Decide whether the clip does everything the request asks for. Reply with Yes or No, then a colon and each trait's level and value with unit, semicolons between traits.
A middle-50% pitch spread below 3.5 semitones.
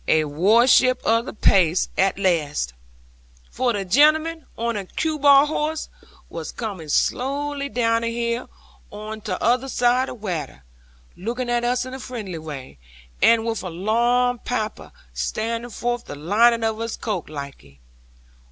No: average, 5.0 semitones